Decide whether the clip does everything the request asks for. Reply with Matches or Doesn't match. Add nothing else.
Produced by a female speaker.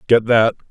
Doesn't match